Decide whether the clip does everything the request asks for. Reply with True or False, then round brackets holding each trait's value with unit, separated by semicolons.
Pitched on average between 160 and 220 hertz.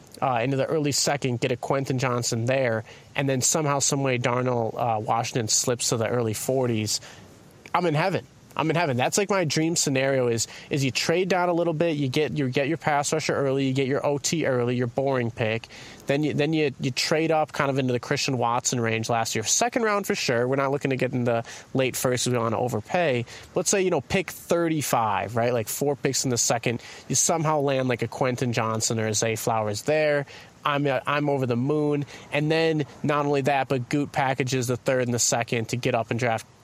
False (135 Hz)